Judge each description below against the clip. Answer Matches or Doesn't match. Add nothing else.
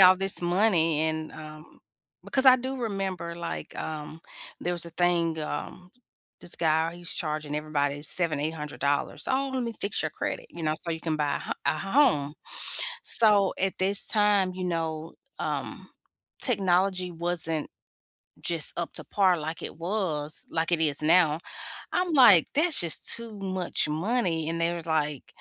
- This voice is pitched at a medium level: Matches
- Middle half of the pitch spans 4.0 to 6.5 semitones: Doesn't match